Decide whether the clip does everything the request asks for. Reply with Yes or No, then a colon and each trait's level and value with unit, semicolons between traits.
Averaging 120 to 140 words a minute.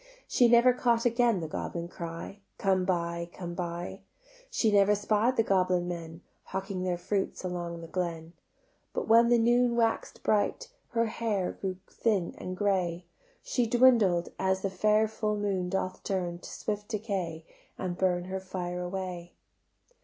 No: average, 155 wpm